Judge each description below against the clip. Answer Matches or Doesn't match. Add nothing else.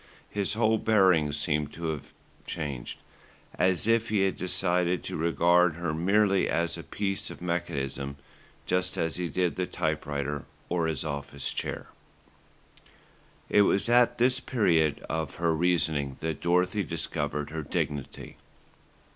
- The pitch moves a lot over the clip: Doesn't match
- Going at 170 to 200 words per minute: Doesn't match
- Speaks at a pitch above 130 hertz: Doesn't match